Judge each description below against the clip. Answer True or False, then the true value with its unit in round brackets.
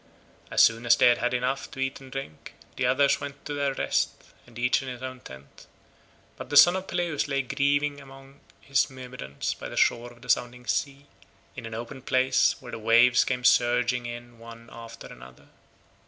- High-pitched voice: False (125 Hz)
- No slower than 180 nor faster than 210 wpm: True (195 wpm)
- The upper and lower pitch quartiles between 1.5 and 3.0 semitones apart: True (2.5 semitones)